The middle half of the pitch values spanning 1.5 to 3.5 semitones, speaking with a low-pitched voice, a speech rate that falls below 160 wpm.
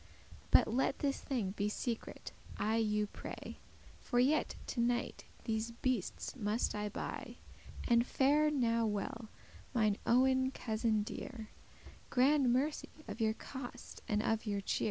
No: average, 3.2 semitones; high, 235 Hz; average, 140 wpm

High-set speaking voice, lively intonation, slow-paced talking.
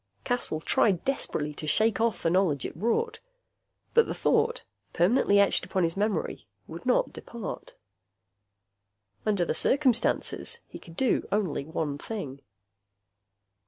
Yes: high, 200 Hz; wide, 6.3 semitones; slow, 130 wpm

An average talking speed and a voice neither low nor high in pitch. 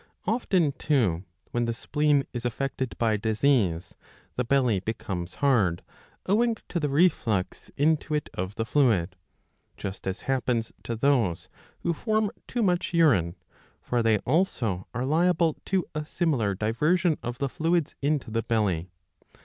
No: average, 150 wpm; low, 130 Hz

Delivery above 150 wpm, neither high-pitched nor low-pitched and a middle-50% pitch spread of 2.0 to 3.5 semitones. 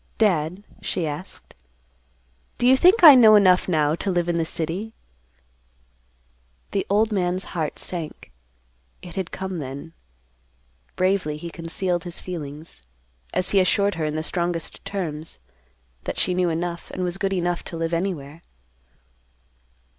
No: average, 145 wpm; medium, 175 Hz; average, 2.8 semitones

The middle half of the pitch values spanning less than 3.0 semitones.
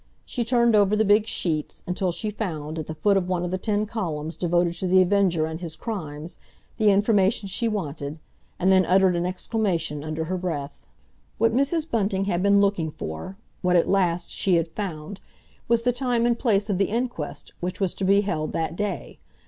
No: average, 4.0 semitones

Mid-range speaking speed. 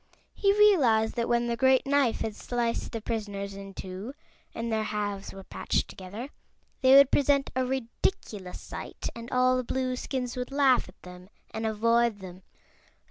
Yes: average, 165 wpm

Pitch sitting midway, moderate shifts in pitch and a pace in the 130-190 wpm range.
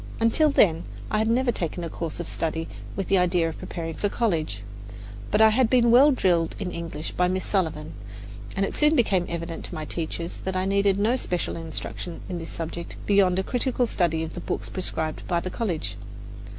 No: medium, 180 Hz; average, 4.3 semitones; fast, 205 wpm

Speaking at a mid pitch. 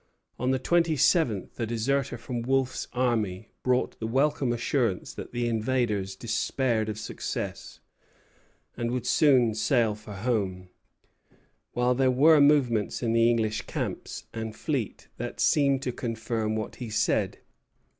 No: low, 120 Hz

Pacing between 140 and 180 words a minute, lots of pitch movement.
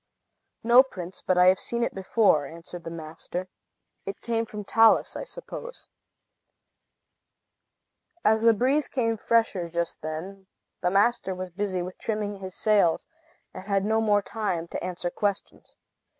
No: average, 150 wpm; average, 3.8 semitones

